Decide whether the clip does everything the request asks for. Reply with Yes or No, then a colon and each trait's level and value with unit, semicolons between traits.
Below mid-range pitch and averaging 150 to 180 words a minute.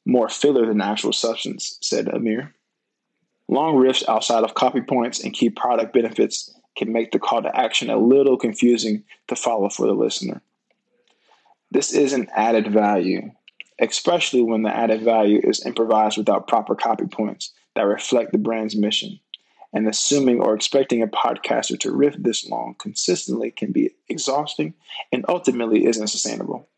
Yes: low, 115 Hz; average, 155 wpm